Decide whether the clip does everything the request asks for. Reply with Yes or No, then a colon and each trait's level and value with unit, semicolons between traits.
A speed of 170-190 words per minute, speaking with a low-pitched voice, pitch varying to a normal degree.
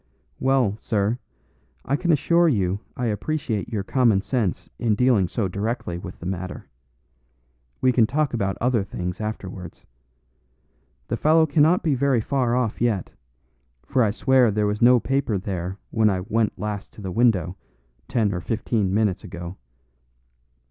No: average, 155 wpm; low, 110 Hz; average, 4.6 semitones